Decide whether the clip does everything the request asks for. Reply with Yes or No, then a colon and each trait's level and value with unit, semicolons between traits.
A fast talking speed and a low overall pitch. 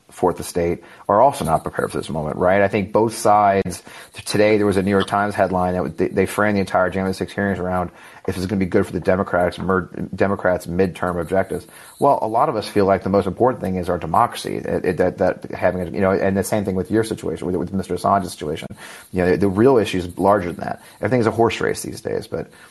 Yes: fast, 250 wpm; very low, 95 Hz